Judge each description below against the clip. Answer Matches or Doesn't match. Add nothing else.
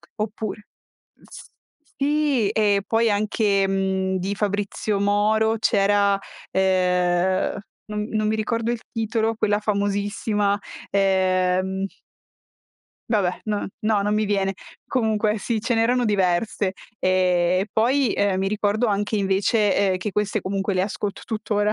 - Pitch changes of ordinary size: Doesn't match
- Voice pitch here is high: Matches